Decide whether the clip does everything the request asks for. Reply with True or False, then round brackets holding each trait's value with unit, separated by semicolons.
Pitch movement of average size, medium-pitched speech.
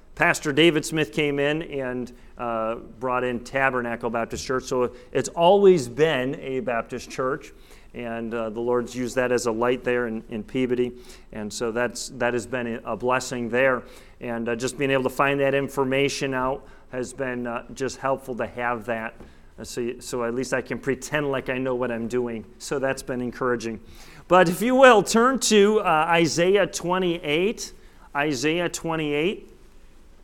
False (3.4 semitones; 130 Hz)